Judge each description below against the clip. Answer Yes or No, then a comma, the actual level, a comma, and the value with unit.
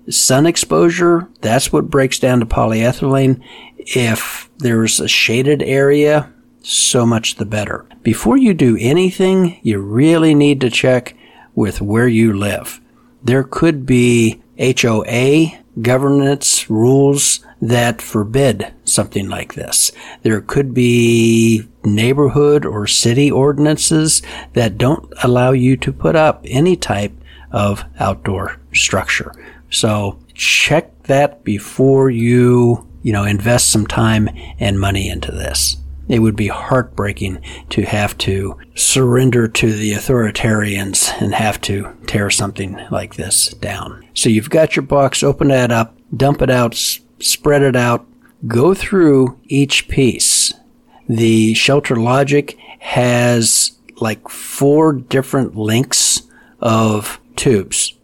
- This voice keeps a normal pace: No, slow, 125 wpm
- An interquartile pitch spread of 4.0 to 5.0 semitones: Yes, average, 4.3 semitones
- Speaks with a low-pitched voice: Yes, low, 120 Hz